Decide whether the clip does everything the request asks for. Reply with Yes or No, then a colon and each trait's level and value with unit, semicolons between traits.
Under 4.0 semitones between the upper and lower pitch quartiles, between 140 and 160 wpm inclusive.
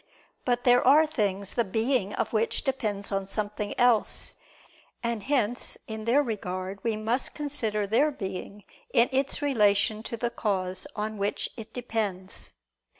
Yes: average, 3.4 semitones; average, 150 wpm